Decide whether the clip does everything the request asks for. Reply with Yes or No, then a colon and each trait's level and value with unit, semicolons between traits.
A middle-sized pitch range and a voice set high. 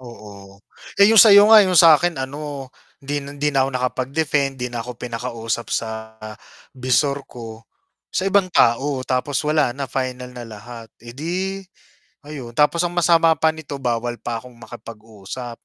No: average, 4.4 semitones; low, 130 Hz